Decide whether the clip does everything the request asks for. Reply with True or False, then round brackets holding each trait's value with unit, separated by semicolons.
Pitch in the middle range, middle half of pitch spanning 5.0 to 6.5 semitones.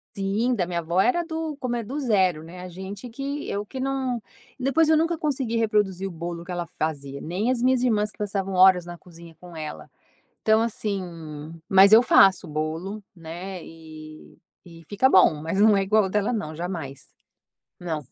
False (195 Hz; 5.5 semitones)